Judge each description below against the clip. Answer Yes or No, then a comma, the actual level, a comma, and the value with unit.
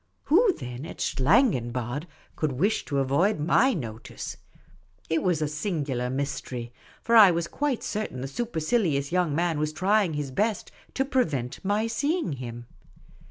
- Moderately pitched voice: Yes, medium, 160 Hz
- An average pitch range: No, wide, 7.9 semitones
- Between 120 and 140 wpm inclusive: No, average, 150 wpm